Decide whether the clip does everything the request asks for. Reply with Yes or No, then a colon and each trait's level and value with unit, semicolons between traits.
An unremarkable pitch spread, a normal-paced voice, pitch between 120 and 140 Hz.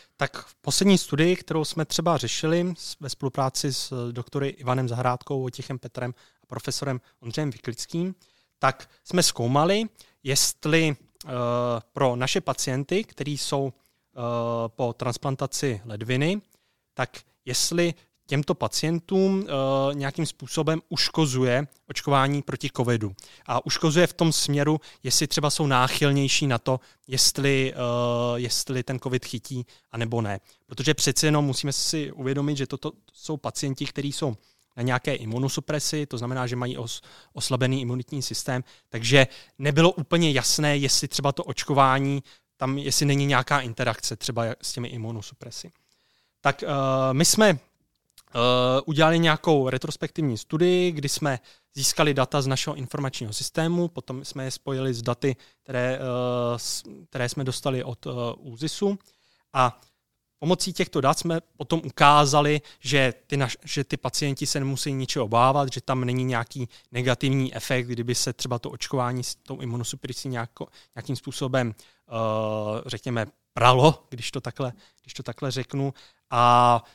Yes: average, 3.0 semitones; average, 140 wpm; low, 135 Hz